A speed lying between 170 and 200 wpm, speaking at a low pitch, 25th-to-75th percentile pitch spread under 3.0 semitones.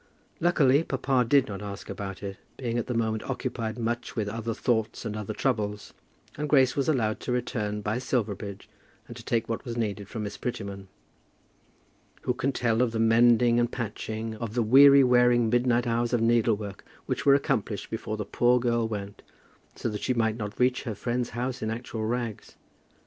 Yes: average, 185 wpm; low, 115 Hz; narrow, 2.4 semitones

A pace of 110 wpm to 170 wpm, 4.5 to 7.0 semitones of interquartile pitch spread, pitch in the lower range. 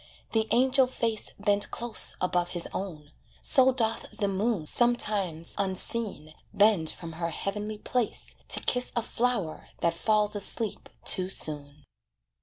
No: slow, 135 wpm; average, 4.9 semitones; high, 205 Hz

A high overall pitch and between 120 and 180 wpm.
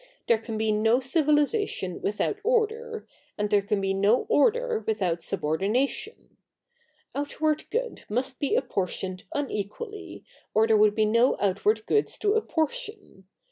Yes: high, 245 Hz; average, 140 wpm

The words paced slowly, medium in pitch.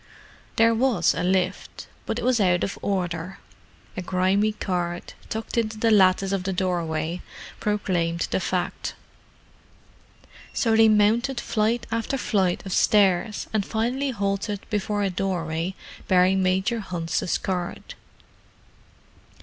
No: slow, 125 wpm; high, 195 Hz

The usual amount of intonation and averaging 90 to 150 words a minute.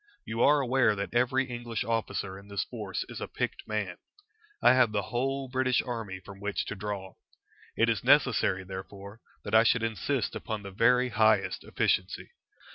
No: average, 3.7 semitones; average, 175 wpm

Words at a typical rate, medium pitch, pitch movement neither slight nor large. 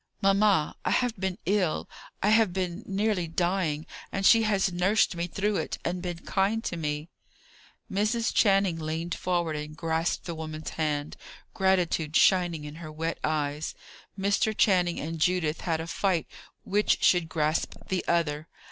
Yes: average, 155 wpm; medium, 175 Hz; average, 3.5 semitones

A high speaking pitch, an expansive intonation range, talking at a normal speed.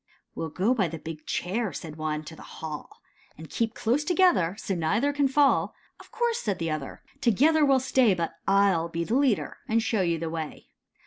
No: high, 195 Hz; wide, 8.1 semitones; fast, 210 wpm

